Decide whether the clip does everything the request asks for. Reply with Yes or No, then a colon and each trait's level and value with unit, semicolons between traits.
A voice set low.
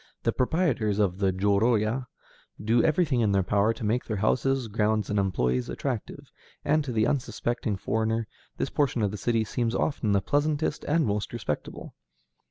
Yes: low, 110 Hz